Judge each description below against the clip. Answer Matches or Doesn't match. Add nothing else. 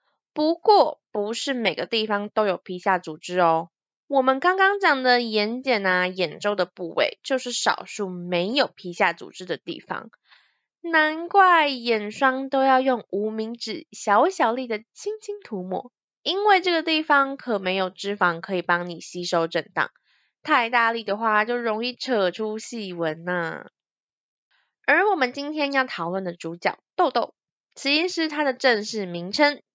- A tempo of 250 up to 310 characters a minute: Doesn't match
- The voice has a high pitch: Matches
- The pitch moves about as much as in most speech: Doesn't match